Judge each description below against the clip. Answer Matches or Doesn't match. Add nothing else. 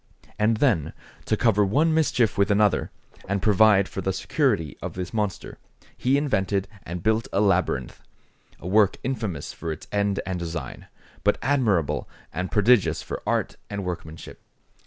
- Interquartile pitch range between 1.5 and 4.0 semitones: Matches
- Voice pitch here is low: Matches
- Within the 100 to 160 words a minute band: Matches